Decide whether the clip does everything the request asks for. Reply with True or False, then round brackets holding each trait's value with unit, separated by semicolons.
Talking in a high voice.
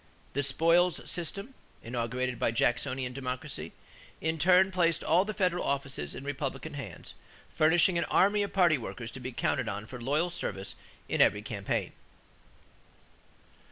False (140 Hz)